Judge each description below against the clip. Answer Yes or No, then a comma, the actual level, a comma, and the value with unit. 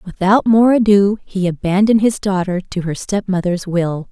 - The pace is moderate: Yes, average, 160 wpm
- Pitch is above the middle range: Yes, high, 195 Hz